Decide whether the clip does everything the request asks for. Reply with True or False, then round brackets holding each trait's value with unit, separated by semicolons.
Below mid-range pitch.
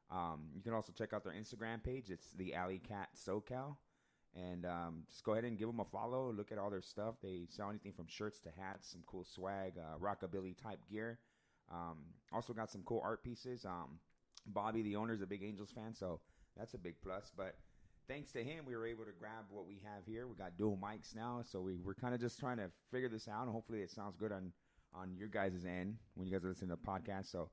True (100 Hz)